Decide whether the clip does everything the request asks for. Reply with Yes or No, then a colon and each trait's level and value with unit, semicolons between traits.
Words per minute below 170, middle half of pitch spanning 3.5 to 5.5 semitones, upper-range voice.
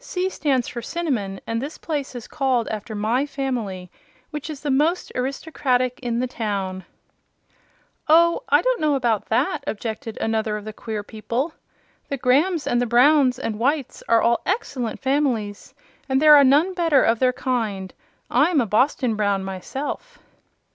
Yes: average, 160 wpm; average, 4.8 semitones; very high, 255 Hz